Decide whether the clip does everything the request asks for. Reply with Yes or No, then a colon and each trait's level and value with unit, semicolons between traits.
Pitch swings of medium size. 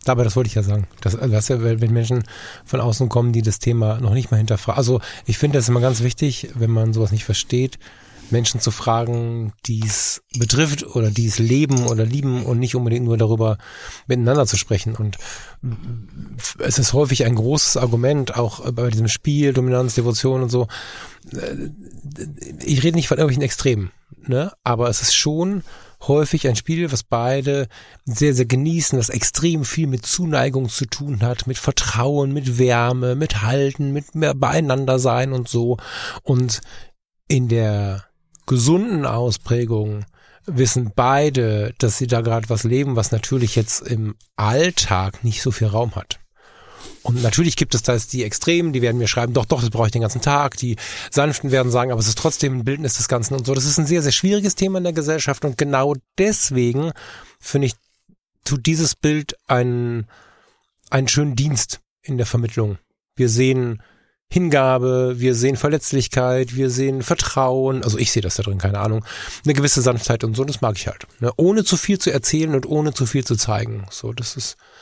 Yes: average, 3.3 semitones